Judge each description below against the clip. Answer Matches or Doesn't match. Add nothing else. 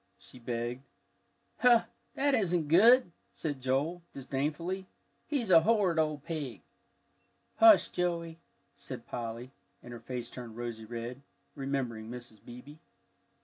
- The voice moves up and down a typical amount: Doesn't match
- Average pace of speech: Doesn't match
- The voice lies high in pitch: Doesn't match